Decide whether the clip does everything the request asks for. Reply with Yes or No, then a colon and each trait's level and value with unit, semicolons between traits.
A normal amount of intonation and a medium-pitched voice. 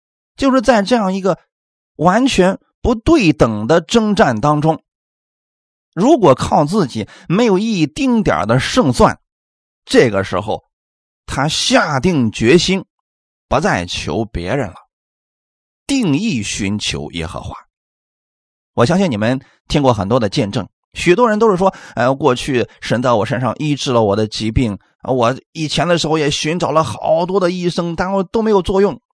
No: wide, 9.0 semitones; medium, 165 Hz